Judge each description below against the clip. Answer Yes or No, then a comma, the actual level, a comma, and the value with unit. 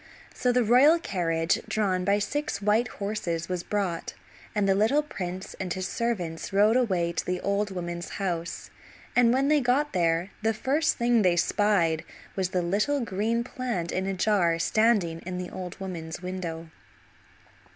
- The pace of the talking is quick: No, average, 165 wpm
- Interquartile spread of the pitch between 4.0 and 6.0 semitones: Yes, average, 4.9 semitones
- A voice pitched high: Yes, high, 195 Hz